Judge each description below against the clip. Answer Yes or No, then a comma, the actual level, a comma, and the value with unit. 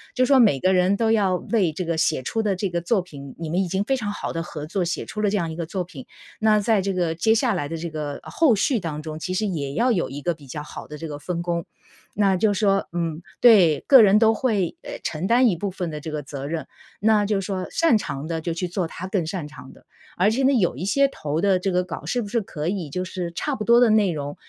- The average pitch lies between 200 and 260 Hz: No, medium, 185 Hz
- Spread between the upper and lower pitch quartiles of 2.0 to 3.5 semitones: No, average, 4.6 semitones